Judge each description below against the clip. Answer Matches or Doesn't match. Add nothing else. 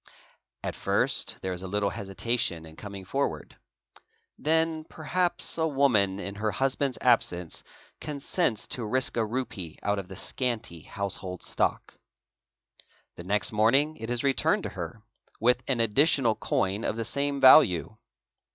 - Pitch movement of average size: Doesn't match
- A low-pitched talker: Matches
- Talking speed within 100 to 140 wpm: Doesn't match